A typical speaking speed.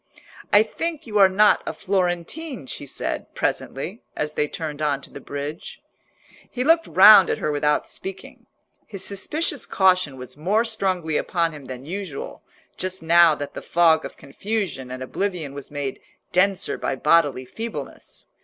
Yes: average, 160 wpm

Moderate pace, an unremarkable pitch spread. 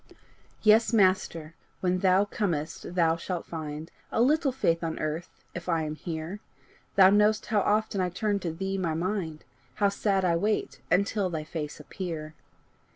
Yes: average, 160 wpm; average, 3.8 semitones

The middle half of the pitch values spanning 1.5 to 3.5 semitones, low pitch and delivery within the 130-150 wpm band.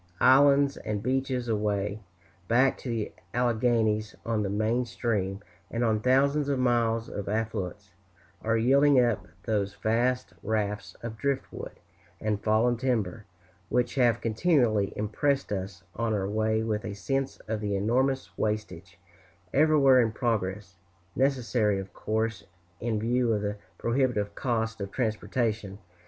Yes: average, 3.2 semitones; low, 110 Hz; average, 140 wpm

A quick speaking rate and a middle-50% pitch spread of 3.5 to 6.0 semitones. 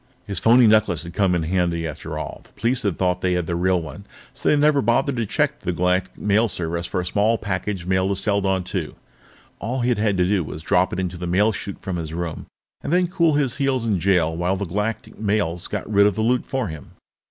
Yes: fast, 245 wpm; average, 4.1 semitones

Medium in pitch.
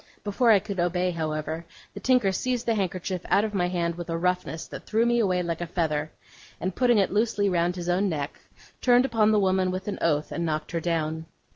Yes: medium, 180 Hz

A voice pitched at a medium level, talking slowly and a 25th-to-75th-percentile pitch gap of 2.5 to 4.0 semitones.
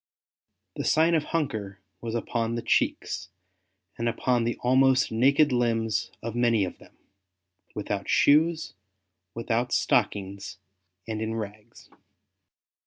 No: low, 115 Hz; slow, 115 wpm; average, 3.0 semitones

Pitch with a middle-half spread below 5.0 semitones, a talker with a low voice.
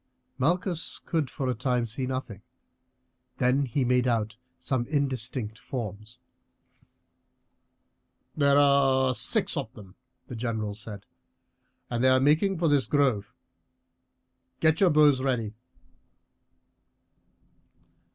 Yes: average, 3.7 semitones; low, 130 Hz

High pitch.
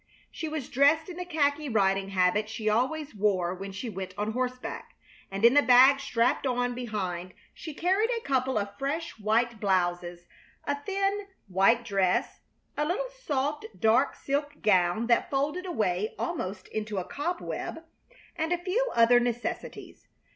Yes: high, 245 Hz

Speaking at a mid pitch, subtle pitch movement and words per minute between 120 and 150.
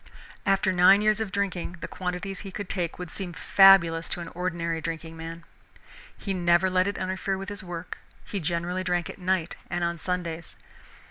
No: medium, 180 Hz; narrow, 2.1 semitones; average, 185 wpm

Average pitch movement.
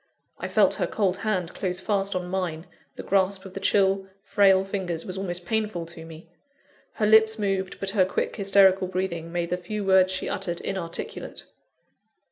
No: narrow, 1.7 semitones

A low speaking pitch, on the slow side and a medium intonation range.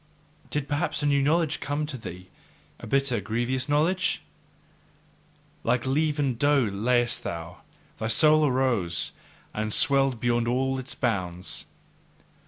Yes: low, 130 Hz; slow, 125 wpm; average, 4.3 semitones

